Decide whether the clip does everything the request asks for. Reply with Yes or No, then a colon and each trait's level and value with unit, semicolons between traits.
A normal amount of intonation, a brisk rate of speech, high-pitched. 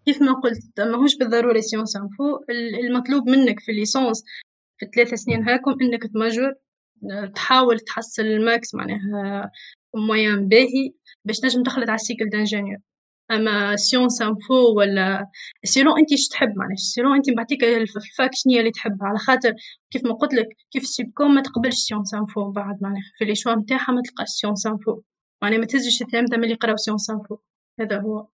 Yes: average, 3.3 semitones; fast, 165 wpm; high, 230 Hz